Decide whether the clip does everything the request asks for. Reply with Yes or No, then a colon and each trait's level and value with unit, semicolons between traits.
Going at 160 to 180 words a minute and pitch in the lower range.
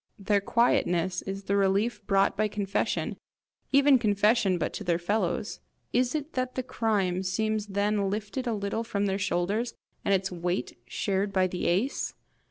No: average, 165 wpm; high, 200 Hz